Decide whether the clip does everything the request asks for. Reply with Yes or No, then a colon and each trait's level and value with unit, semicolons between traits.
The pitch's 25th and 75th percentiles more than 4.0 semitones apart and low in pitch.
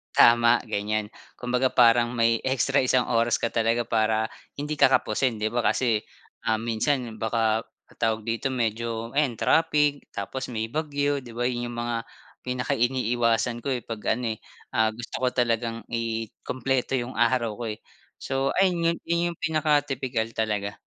No: narrow, 2.6 semitones; low, 120 Hz